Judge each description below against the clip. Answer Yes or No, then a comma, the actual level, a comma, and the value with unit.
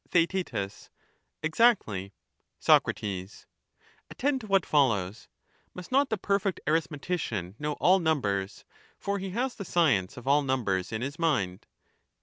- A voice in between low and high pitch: Yes, medium, 150 Hz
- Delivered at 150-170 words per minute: No, slow, 135 wpm